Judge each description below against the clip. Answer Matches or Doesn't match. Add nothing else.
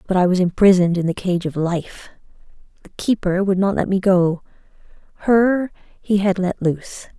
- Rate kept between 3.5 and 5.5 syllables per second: Matches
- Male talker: Doesn't match